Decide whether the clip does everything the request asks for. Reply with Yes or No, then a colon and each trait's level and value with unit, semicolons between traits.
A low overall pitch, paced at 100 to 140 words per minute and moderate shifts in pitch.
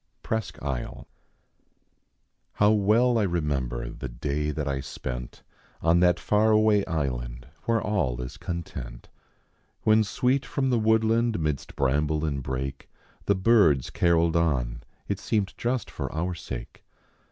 No: very low, 85 Hz; slow, 135 wpm; wide, 7.9 semitones